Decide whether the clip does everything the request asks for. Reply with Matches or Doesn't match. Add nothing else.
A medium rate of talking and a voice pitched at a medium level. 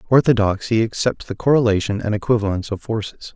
Doesn't match